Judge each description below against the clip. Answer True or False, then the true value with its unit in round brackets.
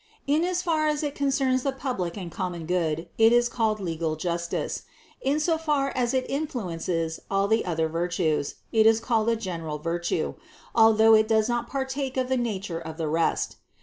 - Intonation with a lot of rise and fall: True (7.6 semitones)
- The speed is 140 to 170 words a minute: False (185 wpm)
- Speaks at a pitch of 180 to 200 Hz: False (220 Hz)